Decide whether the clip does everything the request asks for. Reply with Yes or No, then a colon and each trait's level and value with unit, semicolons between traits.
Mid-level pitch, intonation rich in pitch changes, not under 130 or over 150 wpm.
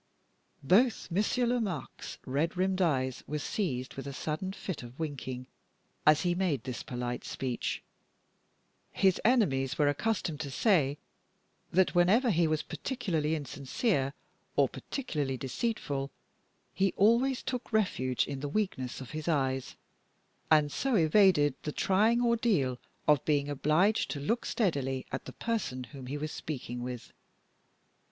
Yes: medium, 155 Hz; wide, 6.8 semitones; average, 140 wpm